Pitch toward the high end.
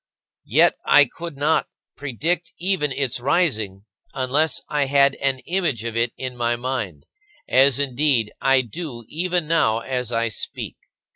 No: low, 135 Hz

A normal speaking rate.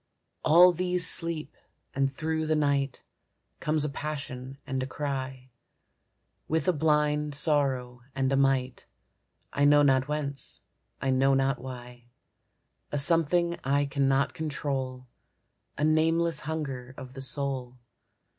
No: slow, 125 wpm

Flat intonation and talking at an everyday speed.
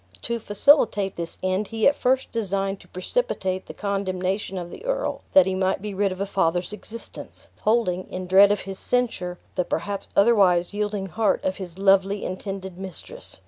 Yes: narrow, 2.2 semitones; average, 180 wpm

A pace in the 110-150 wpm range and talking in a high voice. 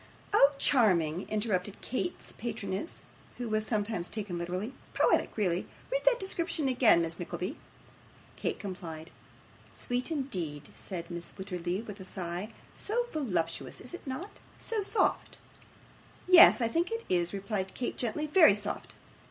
Yes: average, 140 wpm; high, 210 Hz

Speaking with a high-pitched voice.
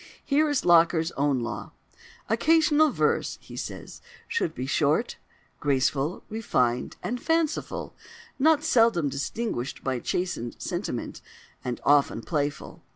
No: medium, 165 Hz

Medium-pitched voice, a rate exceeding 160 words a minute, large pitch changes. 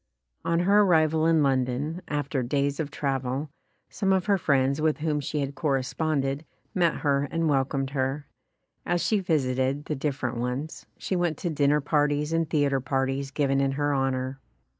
No: medium, 145 Hz; average, 170 wpm; average, 2.8 semitones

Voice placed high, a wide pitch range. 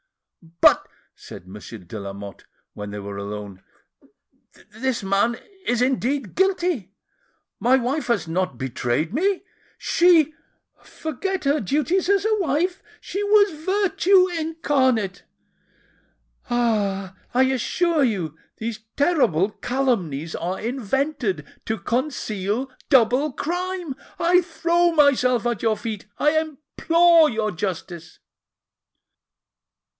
Yes: very high, 255 Hz; wide, 9.0 semitones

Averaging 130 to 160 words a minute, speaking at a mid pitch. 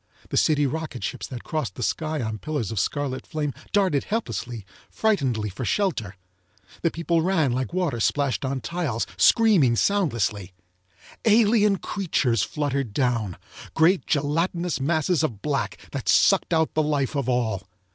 Yes: average, 145 wpm; medium, 145 Hz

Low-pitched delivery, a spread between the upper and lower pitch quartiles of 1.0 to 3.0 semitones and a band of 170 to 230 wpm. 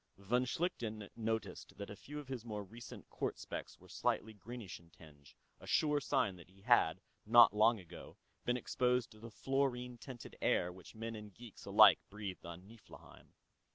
No: low, 110 Hz; average, 3.8 semitones; average, 180 wpm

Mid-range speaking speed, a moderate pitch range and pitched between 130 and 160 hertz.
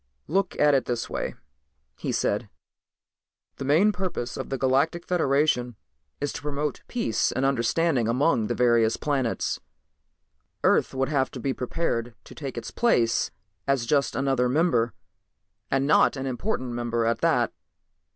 Yes: average, 150 wpm; average, 3.7 semitones; low, 135 Hz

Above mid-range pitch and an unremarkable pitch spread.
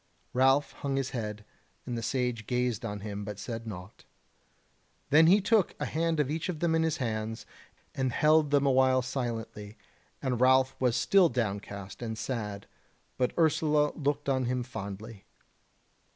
No: low, 125 Hz; average, 4.6 semitones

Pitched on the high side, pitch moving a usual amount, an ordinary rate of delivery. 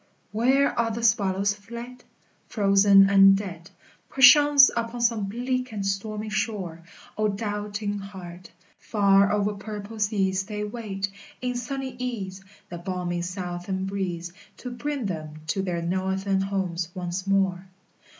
No: high, 200 Hz; average, 3.0 semitones; slow, 130 wpm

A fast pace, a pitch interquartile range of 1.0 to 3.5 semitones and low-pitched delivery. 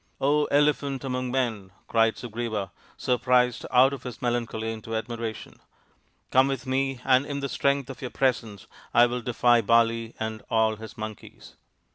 No: average, 165 wpm; average, 2.8 semitones; low, 120 Hz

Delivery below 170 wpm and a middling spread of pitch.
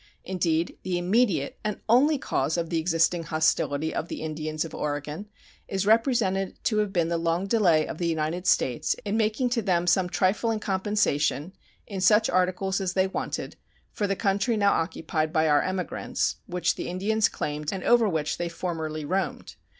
No: average, 175 wpm; average, 4.1 semitones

